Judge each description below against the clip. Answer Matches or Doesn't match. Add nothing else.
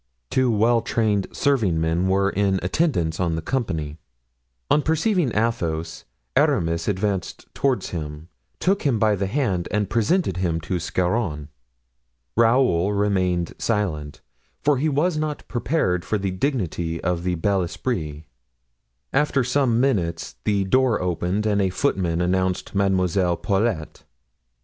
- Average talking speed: Doesn't match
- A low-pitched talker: Matches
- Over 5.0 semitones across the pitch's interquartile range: Matches